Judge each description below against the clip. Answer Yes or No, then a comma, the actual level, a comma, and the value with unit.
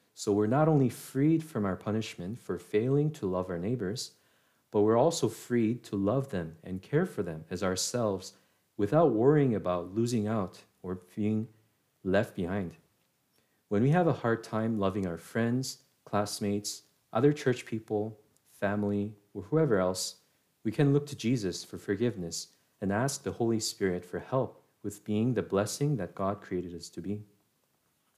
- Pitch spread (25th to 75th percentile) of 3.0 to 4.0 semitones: No, average, 4.6 semitones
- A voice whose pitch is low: Yes, low, 105 Hz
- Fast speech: No, average, 165 wpm